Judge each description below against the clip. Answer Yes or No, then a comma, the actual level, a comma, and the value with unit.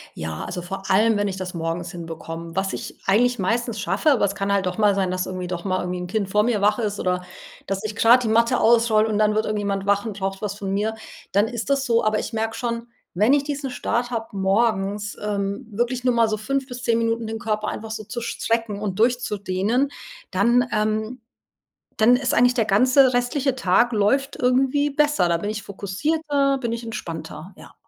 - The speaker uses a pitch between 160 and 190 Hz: No, high, 215 Hz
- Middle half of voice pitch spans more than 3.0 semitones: Yes, average, 3.7 semitones